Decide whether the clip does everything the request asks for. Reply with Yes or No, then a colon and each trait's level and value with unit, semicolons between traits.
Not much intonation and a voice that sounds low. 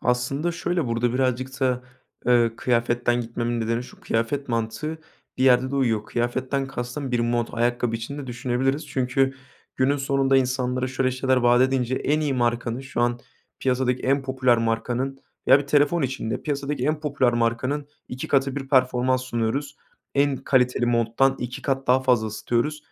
Yes: narrow, 2.0 semitones; low, 130 Hz